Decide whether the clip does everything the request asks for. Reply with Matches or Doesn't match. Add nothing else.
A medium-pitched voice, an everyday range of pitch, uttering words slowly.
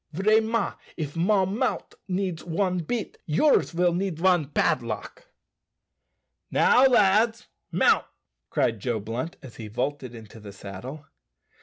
Doesn't match